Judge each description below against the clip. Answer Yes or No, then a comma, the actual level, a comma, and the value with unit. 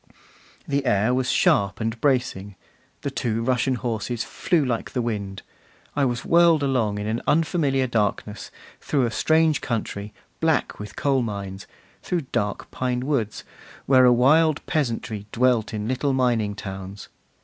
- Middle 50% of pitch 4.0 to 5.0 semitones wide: Yes, average, 4.4 semitones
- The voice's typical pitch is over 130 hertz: No, low, 120 Hz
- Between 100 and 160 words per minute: Yes, average, 150 wpm